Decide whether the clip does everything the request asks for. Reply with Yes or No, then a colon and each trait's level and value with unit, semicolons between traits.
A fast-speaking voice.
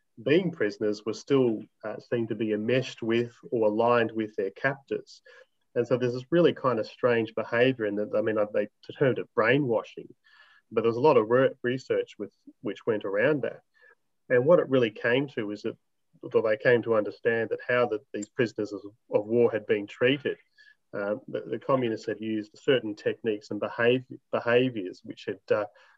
No: average, 190 wpm